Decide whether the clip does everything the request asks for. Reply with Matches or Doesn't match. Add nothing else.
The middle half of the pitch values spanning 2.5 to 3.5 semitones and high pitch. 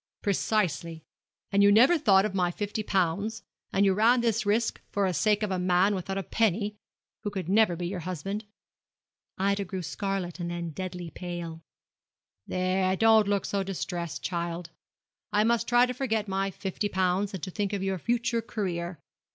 Matches